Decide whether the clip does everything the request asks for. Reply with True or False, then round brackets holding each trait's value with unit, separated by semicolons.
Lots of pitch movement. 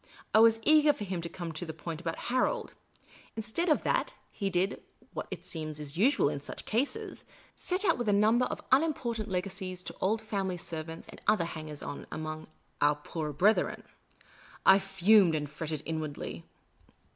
True (5.9 semitones)